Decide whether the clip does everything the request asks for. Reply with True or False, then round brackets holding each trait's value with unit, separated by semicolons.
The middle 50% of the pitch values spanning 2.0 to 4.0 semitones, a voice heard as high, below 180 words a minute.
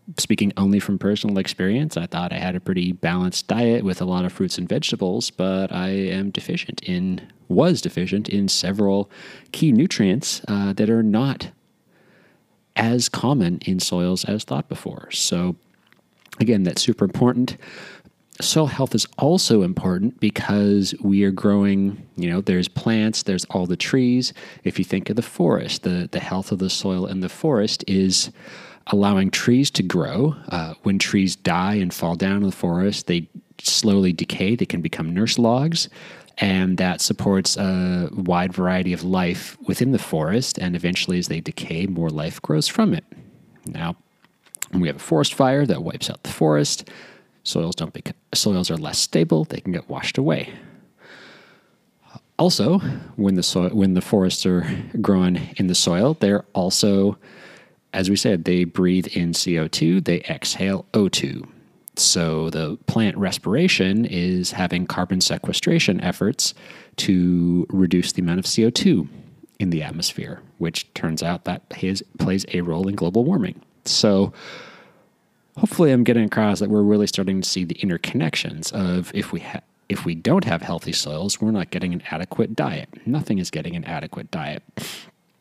False (3.2 semitones; 95 Hz; 165 wpm)